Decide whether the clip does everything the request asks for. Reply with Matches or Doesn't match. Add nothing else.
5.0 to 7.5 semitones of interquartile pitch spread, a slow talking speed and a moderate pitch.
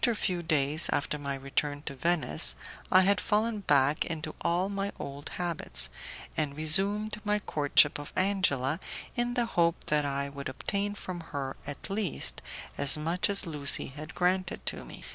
Doesn't match